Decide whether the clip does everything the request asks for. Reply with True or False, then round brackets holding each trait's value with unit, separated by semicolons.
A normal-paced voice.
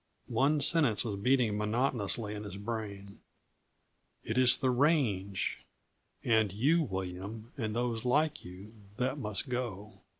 False (130 wpm)